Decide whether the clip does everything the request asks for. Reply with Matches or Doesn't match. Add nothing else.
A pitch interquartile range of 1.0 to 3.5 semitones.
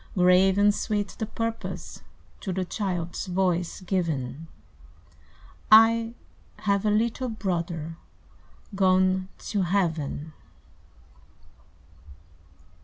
Matches